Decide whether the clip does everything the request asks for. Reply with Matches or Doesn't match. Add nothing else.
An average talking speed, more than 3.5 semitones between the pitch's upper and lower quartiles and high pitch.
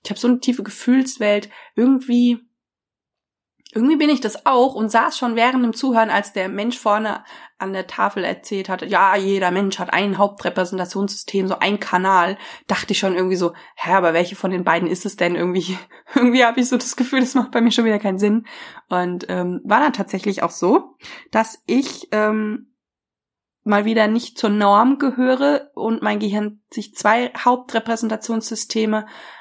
Matches